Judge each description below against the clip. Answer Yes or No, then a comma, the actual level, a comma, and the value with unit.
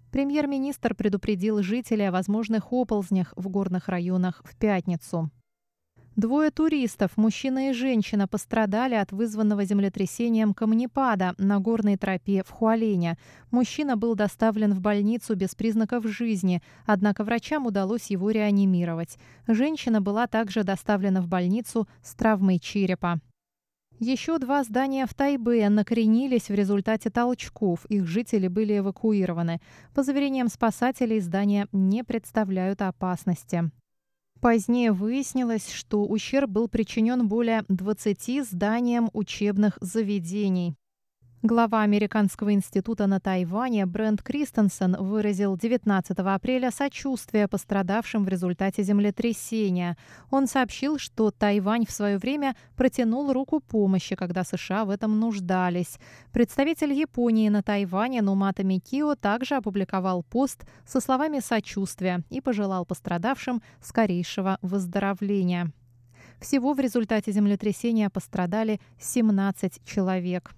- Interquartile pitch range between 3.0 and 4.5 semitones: Yes, average, 3.6 semitones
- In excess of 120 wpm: No, average, 115 wpm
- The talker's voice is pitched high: Yes, high, 210 Hz